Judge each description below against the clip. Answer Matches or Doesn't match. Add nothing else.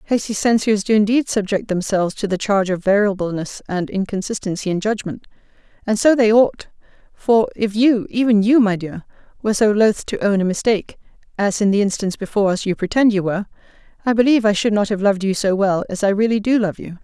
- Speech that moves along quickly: Matches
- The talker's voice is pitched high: Matches